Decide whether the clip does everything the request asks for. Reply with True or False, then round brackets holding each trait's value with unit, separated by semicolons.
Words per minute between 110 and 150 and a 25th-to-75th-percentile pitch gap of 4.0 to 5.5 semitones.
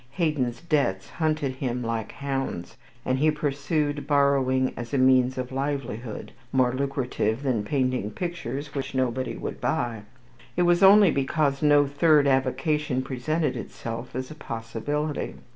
False (145 wpm; 2.9 semitones)